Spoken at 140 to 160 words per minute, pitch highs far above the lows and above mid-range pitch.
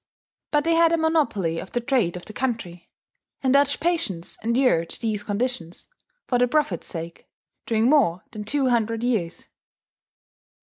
Yes: average, 150 wpm; wide, 6.8 semitones; high, 235 Hz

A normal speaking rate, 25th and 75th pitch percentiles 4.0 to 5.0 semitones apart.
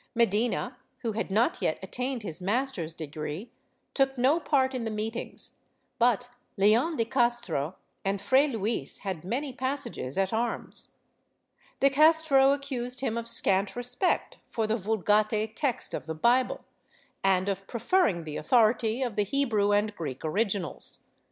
Yes: average, 145 wpm; average, 4.7 semitones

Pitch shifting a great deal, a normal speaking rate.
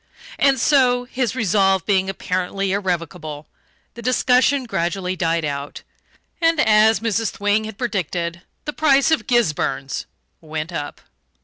No: wide, 6.4 semitones; slow, 125 wpm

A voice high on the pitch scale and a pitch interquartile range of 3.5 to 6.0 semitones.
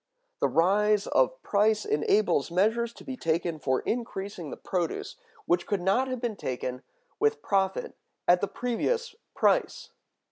Yes: high, 200 Hz; average, 5.1 semitones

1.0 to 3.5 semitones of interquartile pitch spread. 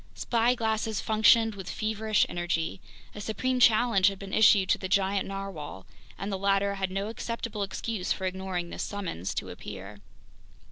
Yes: narrow, 2.6 semitones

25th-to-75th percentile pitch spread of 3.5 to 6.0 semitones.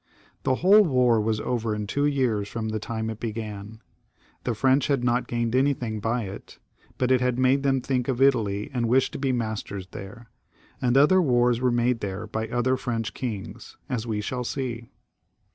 No: average, 2.8 semitones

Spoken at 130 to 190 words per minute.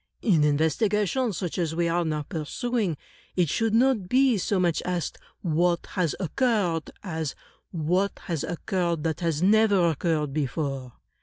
Yes: average, 150 wpm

